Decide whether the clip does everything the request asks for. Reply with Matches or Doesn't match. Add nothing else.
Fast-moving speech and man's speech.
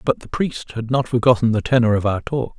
Matches